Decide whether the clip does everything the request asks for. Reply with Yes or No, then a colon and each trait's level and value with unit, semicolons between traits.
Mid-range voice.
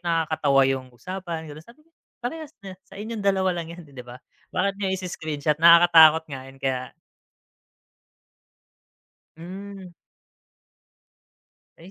Yes: medium, 170 Hz